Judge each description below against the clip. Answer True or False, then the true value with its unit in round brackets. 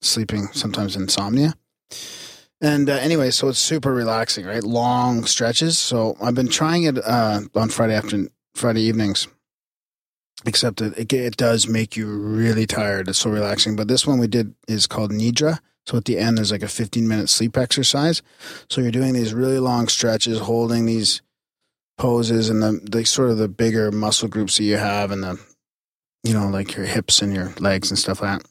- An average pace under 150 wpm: False (190 wpm)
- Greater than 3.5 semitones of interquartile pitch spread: False (2.6 semitones)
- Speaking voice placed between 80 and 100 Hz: False (115 Hz)